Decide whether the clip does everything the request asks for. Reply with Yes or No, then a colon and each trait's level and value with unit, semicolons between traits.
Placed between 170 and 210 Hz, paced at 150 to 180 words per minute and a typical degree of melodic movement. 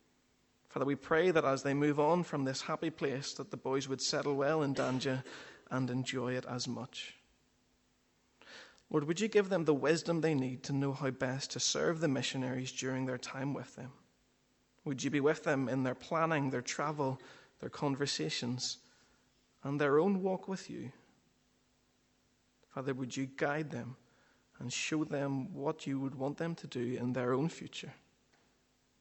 No: low, 135 Hz; average, 175 wpm; average, 3.0 semitones